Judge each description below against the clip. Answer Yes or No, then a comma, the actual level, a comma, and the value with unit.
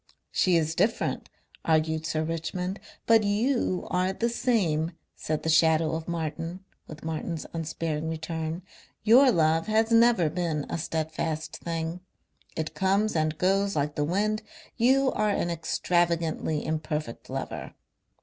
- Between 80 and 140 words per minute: Yes, slow, 135 wpm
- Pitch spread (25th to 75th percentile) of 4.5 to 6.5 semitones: No, average, 3.8 semitones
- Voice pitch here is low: No, medium, 165 Hz